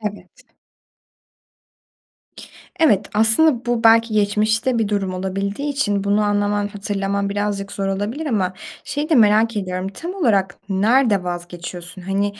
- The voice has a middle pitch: No, high, 205 Hz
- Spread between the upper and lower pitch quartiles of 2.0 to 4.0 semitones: Yes, narrow, 2.6 semitones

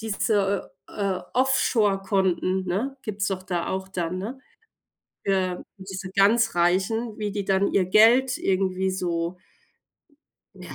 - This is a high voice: Yes, high, 195 Hz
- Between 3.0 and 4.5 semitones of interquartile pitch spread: No, narrow, 2.4 semitones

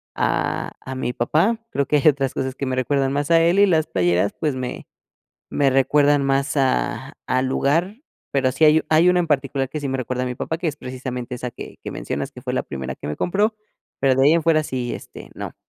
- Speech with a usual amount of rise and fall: Yes, average, 3.3 semitones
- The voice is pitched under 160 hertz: Yes, low, 135 Hz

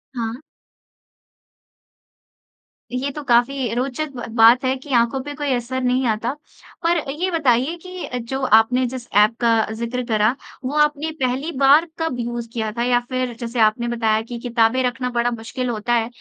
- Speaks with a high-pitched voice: Yes, high, 245 Hz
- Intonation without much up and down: Yes, narrow, 2.3 semitones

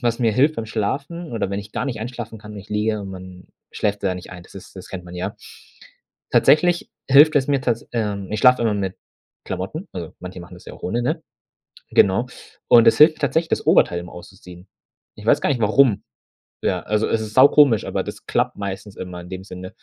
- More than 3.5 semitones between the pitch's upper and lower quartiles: Yes, average, 5.1 semitones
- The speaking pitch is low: Yes, low, 105 Hz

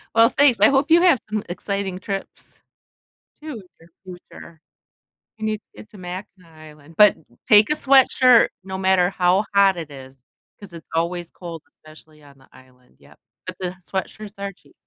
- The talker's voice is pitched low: No, high, 190 Hz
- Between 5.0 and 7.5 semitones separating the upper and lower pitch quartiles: No, average, 4.3 semitones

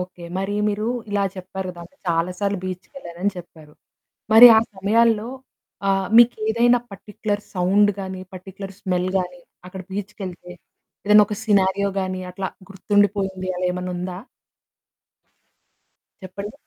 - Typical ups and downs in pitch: No, narrow, 2.1 semitones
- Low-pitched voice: No, high, 190 Hz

